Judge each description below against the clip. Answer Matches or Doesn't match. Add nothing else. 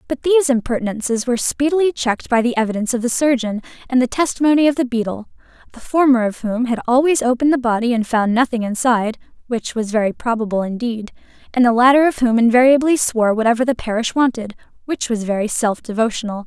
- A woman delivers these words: Matches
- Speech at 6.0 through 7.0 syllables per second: Matches